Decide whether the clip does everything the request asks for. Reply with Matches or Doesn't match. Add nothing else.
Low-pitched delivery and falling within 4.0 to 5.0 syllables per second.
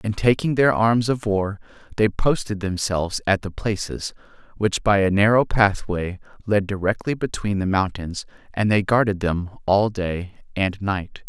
Matches